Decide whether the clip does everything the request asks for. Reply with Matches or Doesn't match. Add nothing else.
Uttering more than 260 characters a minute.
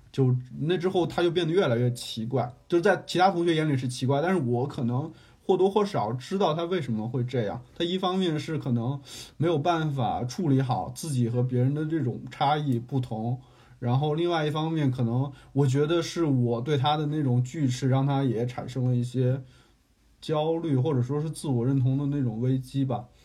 Matches